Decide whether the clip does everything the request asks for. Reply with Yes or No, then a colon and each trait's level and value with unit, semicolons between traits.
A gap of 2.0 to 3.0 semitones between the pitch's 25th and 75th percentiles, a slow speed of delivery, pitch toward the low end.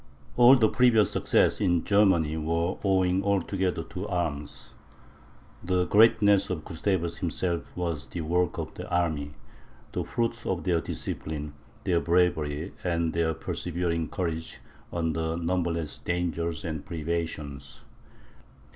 Yes: narrow, 2.4 semitones; slow, 120 wpm; very low, 85 Hz